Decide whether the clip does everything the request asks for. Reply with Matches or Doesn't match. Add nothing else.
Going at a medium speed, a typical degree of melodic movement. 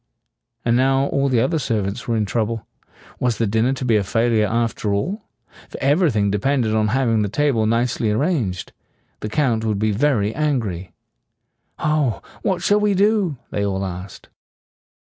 Matches